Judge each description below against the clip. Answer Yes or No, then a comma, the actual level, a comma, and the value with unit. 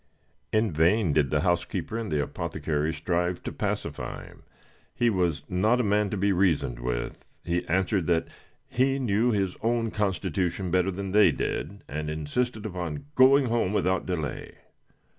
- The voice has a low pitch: Yes, very low, 95 Hz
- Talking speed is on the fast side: No, average, 160 wpm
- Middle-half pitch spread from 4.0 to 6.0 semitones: Yes, average, 4.7 semitones